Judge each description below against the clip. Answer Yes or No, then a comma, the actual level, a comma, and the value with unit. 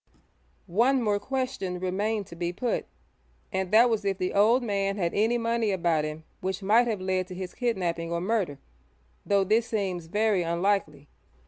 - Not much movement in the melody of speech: No, average, 3.8 semitones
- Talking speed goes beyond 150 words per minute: Yes, average, 175 wpm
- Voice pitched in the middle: No, high, 195 Hz